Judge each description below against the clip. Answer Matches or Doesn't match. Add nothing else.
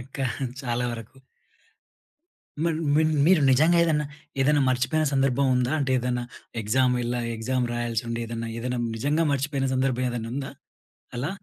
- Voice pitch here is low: Matches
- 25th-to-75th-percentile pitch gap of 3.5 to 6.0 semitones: Doesn't match